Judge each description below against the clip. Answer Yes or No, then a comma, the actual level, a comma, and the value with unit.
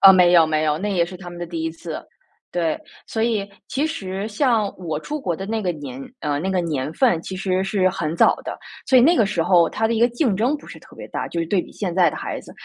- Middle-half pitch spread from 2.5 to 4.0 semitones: No, average, 4.7 semitones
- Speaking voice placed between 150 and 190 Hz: Yes, medium, 185 Hz